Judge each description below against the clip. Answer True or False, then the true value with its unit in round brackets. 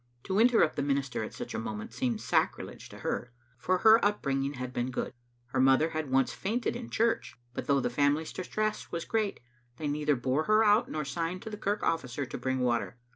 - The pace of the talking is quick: True (220 wpm)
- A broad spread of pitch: True (7.8 semitones)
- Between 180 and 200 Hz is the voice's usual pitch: False (145 Hz)